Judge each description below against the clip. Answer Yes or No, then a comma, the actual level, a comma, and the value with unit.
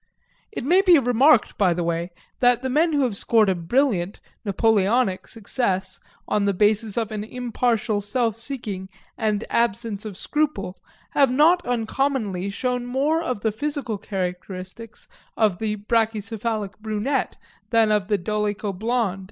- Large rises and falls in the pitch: No, average, 3.7 semitones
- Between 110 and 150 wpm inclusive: Yes, average, 145 wpm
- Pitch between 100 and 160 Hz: No, high, 220 Hz